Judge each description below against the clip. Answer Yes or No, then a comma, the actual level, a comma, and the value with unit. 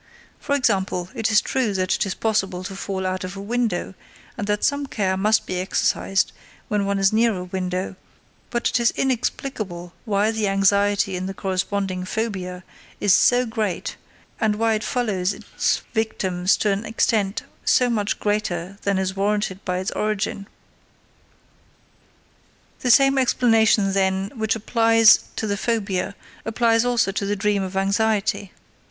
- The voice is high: Yes, high, 205 Hz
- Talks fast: No, average, 160 wpm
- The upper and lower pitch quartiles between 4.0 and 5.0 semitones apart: No, average, 2.7 semitones